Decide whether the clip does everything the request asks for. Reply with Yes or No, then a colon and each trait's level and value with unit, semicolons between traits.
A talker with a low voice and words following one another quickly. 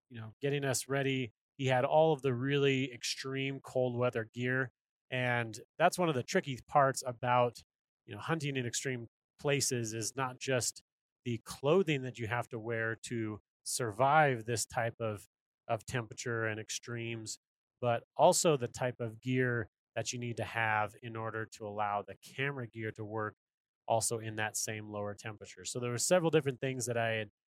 No: low, 120 Hz; average, 180 wpm